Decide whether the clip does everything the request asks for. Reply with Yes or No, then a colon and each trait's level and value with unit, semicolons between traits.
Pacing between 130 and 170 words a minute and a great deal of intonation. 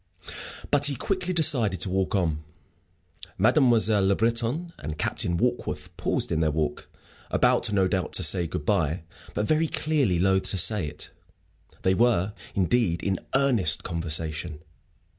Yes: average, 145 wpm; wide, 6.3 semitones